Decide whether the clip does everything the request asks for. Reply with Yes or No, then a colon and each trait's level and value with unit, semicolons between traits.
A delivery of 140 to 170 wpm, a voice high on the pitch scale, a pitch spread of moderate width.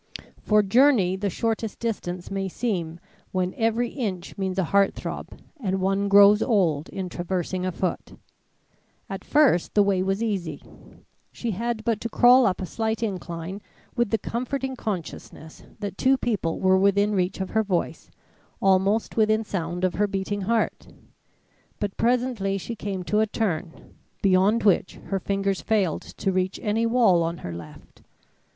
Yes: average, 160 wpm; high, 195 Hz; average, 3.2 semitones